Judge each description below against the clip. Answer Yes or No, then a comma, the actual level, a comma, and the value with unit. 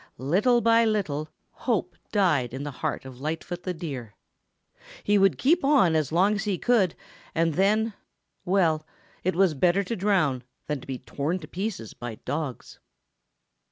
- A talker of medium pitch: Yes, medium, 175 Hz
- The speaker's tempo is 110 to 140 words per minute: No, average, 165 wpm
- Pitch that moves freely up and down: Yes, wide, 5.8 semitones